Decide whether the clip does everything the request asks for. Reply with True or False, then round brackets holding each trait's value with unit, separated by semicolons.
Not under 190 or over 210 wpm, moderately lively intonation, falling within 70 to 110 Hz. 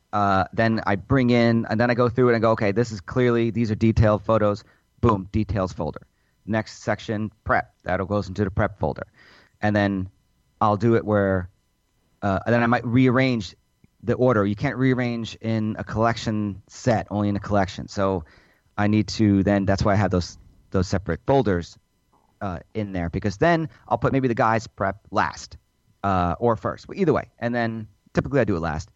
True (200 wpm; 3.1 semitones; 105 Hz)